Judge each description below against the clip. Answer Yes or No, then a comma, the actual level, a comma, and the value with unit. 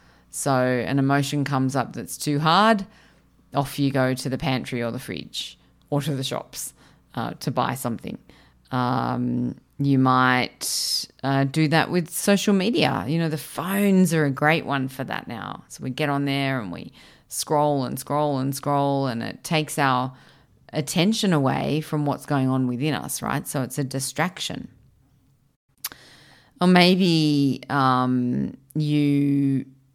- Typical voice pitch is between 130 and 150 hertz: Yes, medium, 140 Hz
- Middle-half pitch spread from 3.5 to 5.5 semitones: No, average, 2.8 semitones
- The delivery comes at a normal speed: Yes, average, 155 wpm